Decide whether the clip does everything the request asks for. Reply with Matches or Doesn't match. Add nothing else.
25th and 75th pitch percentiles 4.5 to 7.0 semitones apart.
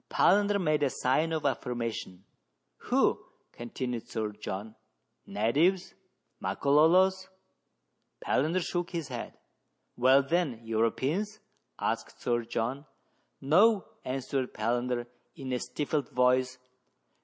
Matches